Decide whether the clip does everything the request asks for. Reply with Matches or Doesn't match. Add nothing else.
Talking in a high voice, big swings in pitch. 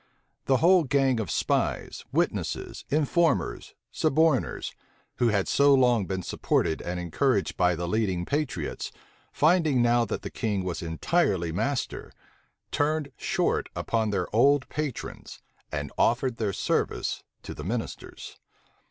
Doesn't match